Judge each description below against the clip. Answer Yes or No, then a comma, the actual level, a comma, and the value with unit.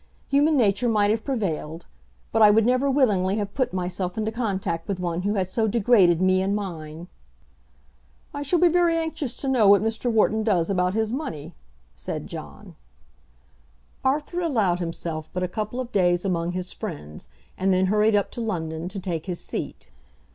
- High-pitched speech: Yes, high, 205 Hz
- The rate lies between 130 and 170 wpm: No, average, 180 wpm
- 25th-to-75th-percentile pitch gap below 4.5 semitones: No, average, 4.8 semitones